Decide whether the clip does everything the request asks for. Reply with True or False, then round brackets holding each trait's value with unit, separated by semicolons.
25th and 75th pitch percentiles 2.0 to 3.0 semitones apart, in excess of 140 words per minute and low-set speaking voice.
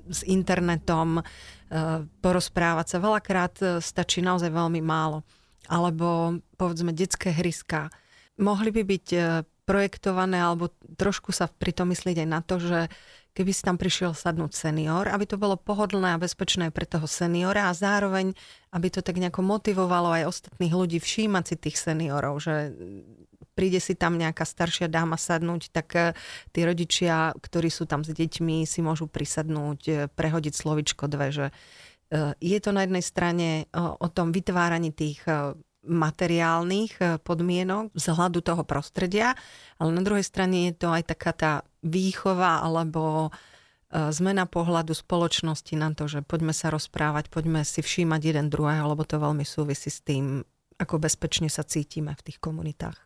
False (2.5 semitones; 150 wpm; 170 Hz)